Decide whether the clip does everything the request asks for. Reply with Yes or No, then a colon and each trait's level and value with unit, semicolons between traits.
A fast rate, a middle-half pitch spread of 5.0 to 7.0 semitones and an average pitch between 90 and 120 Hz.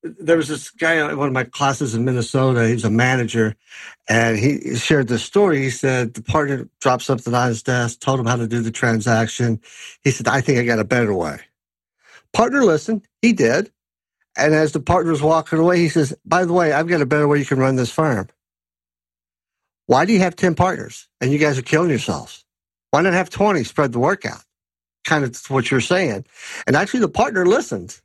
No: fast, 210 wpm; average, 5.3 semitones; low, 135 Hz